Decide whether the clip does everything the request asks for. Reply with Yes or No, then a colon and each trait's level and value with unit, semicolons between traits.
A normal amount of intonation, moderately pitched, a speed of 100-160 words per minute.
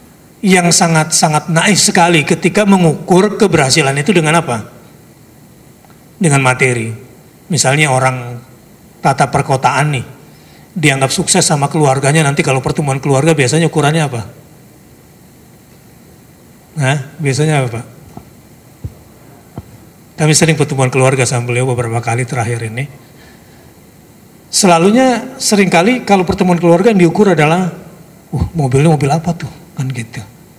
Yes: average, 4.7 semitones; medium, 155 Hz; average, 115 wpm